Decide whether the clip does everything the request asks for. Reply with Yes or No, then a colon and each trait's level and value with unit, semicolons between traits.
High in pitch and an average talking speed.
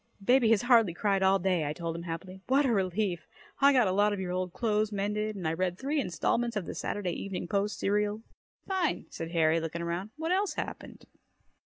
No: high, 195 Hz; fast, 210 wpm